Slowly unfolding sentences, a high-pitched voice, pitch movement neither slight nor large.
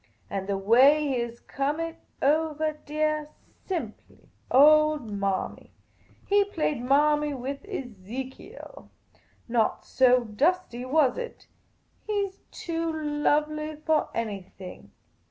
Yes: slow, 115 wpm; very high, 295 Hz; average, 4.2 semitones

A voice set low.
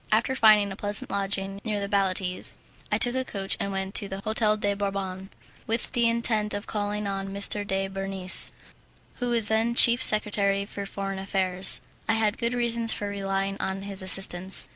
No: high, 200 Hz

